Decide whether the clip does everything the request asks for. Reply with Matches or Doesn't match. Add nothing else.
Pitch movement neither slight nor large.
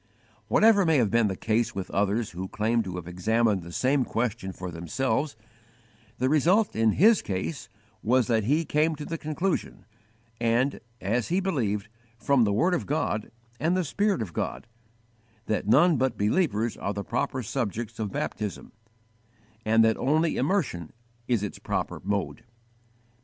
Doesn't match